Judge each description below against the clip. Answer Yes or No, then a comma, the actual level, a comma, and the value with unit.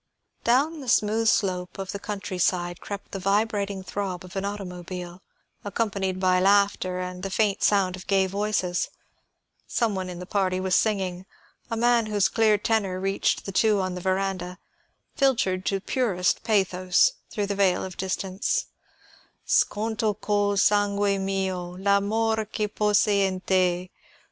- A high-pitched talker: Yes, high, 195 Hz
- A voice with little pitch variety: Yes, narrow, 2.1 semitones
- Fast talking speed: No, average, 150 wpm